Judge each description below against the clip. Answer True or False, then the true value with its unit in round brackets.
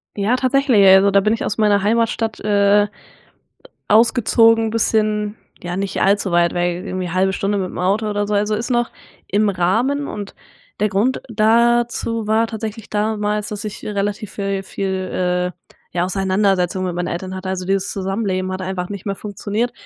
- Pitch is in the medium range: False (205 Hz)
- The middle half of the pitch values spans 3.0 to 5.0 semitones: False (2.5 semitones)